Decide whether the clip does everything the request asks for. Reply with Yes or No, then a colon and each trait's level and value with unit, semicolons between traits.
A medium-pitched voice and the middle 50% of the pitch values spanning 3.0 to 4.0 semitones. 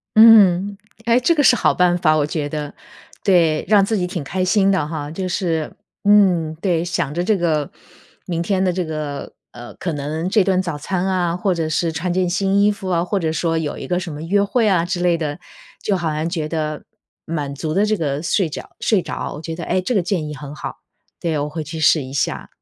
Yes: medium, 170 Hz; average, 3.6 semitones